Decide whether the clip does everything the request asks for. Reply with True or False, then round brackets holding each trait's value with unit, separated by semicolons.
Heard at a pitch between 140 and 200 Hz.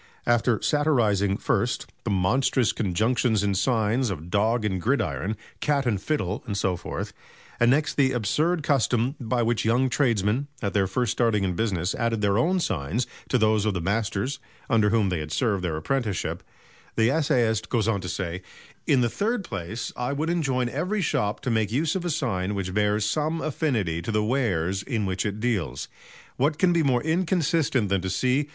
False (115 Hz)